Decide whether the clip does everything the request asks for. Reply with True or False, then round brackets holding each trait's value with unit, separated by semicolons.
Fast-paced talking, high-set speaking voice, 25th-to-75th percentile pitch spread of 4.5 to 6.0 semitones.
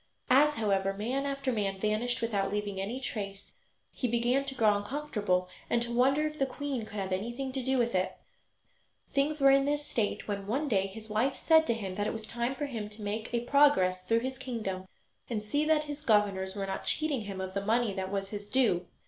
True (220 wpm; 225 Hz; 5.0 semitones)